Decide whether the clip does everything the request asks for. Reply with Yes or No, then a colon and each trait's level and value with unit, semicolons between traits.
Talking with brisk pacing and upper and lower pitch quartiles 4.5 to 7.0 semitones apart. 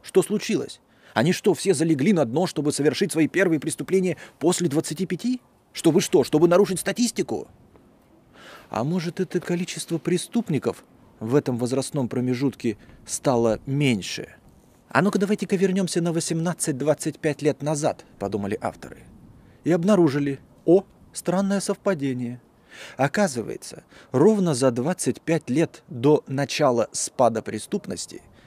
No: average, 120 wpm; average, 5.0 semitones